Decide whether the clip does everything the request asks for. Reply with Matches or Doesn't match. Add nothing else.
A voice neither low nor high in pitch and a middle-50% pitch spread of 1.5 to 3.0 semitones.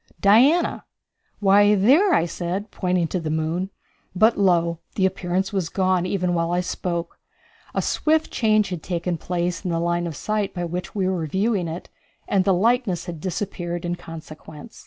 Matches